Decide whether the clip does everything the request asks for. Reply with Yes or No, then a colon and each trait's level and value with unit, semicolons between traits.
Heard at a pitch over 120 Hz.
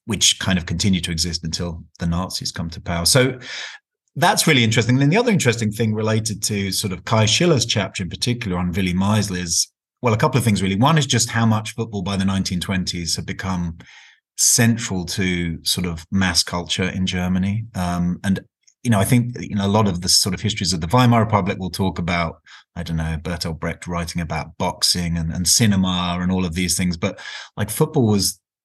No: very low, 95 Hz